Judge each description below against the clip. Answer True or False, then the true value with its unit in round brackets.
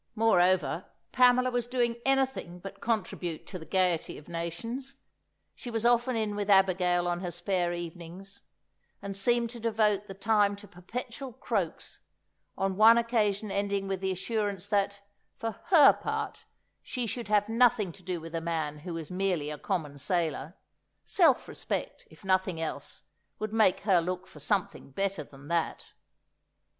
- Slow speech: False (160 wpm)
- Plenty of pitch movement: False (4.4 semitones)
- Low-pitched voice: False (195 Hz)